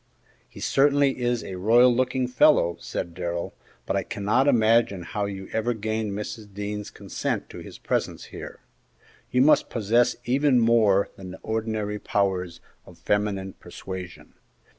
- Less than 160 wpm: Yes, average, 145 wpm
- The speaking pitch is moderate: No, low, 110 Hz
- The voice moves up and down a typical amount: Yes, average, 3.8 semitones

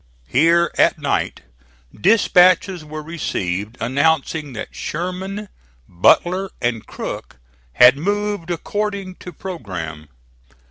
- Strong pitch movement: Yes, wide, 7.2 semitones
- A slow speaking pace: Yes, slow, 95 wpm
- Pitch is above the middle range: No, medium, 165 Hz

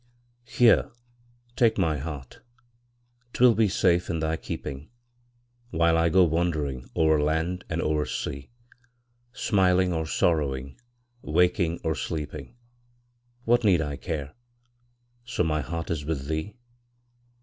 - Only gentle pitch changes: No, average, 3.0 semitones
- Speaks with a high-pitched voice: No, very low, 80 Hz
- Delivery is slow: Yes, slow, 120 wpm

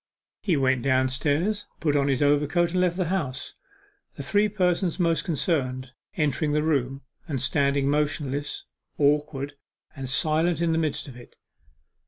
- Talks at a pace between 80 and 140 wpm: No, average, 150 wpm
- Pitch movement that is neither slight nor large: Yes, average, 3.6 semitones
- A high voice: No, medium, 145 Hz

